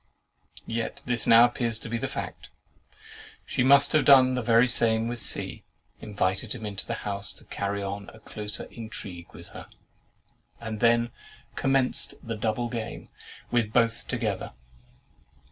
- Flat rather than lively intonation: Yes, narrow, 2.2 semitones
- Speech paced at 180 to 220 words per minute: No, average, 150 wpm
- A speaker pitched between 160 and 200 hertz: No, low, 115 Hz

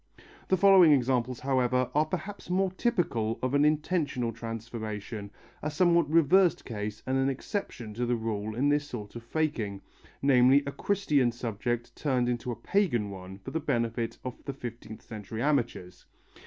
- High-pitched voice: No, low, 125 Hz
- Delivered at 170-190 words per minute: No, average, 160 wpm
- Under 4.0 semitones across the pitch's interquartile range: No, average, 4.9 semitones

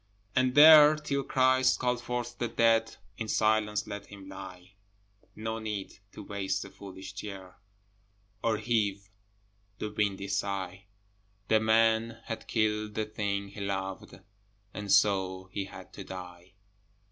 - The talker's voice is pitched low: Yes, low, 105 Hz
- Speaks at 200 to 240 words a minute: No, slow, 135 wpm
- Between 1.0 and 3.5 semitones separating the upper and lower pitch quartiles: Yes, narrow, 2.6 semitones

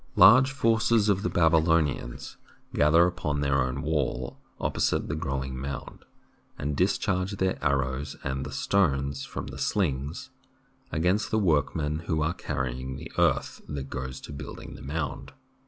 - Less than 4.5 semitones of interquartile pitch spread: No, average, 5.1 semitones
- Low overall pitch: Yes, very low, 75 Hz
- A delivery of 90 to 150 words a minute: Yes, average, 145 wpm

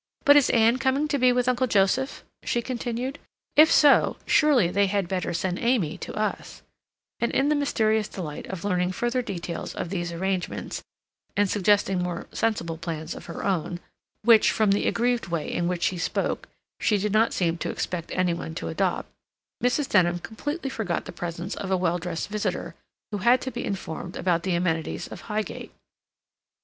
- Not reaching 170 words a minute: No, average, 180 wpm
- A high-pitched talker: Yes, high, 200 Hz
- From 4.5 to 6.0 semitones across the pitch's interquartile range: Yes, wide, 5.5 semitones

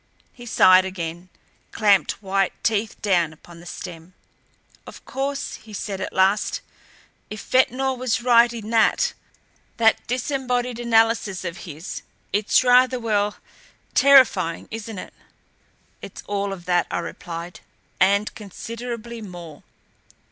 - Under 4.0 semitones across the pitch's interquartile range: No, average, 4.4 semitones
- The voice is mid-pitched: No, high, 210 Hz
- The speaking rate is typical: No, slow, 125 wpm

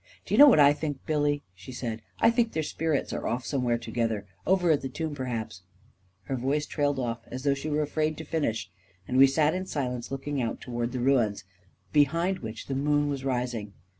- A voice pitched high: No, low, 135 Hz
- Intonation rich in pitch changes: No, average, 3.8 semitones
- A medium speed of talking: No, fast, 225 wpm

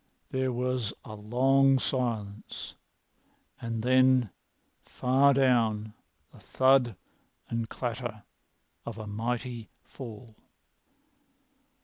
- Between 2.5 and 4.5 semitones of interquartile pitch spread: Yes, average, 2.8 semitones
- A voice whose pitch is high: No, low, 120 Hz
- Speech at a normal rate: No, slow, 85 wpm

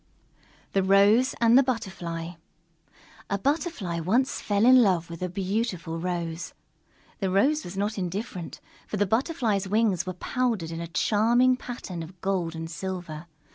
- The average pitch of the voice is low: No, high, 195 Hz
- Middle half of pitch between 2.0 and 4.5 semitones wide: No, average, 5.0 semitones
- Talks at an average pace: Yes, average, 155 wpm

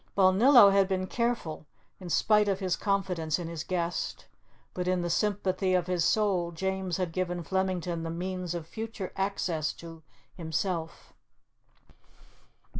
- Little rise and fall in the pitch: Yes, narrow, 2.3 semitones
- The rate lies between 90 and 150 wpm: Yes, average, 140 wpm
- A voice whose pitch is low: No, medium, 185 Hz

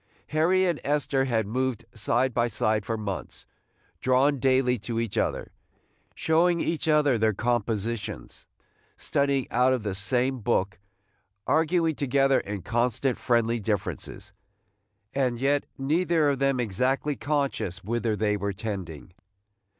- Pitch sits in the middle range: No, low, 125 Hz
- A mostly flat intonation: No, average, 4.5 semitones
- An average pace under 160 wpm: Yes, slow, 135 wpm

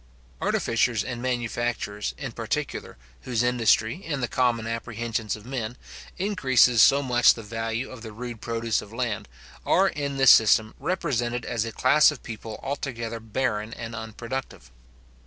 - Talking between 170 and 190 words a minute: No, average, 150 wpm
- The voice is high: No, low, 120 Hz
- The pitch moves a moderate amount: No, narrow, 2.3 semitones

